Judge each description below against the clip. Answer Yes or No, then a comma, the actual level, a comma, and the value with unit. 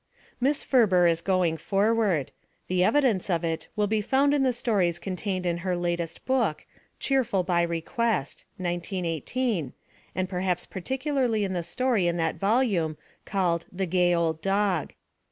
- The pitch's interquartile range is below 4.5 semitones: No, average, 4.8 semitones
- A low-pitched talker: No, medium, 185 Hz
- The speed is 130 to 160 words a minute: Yes, average, 155 wpm